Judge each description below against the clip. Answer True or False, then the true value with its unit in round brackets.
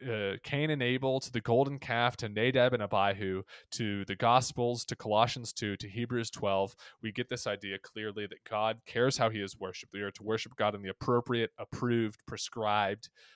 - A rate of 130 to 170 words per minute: False (195 wpm)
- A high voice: False (115 Hz)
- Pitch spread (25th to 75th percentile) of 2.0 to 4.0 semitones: True (2.9 semitones)